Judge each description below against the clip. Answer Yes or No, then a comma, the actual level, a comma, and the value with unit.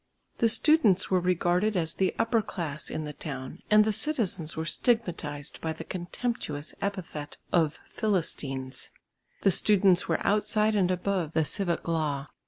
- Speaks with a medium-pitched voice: Yes, medium, 180 Hz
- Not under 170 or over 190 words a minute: No, average, 150 wpm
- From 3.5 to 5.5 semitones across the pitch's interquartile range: Yes, average, 5.1 semitones